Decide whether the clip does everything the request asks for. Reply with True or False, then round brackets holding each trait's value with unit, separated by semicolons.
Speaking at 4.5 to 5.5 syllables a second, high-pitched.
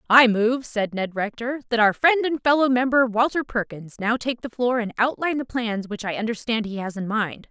True (5.2 syllables/s; 235 Hz)